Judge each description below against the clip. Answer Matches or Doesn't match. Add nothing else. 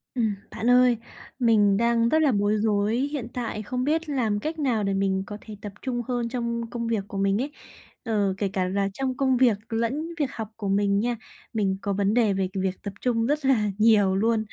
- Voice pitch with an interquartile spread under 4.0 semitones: Matches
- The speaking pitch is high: Matches